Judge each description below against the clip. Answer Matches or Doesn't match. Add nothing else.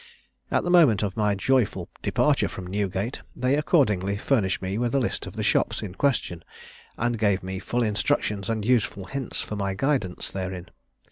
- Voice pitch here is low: Matches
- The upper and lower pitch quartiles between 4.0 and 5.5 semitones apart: Matches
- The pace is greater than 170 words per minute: Matches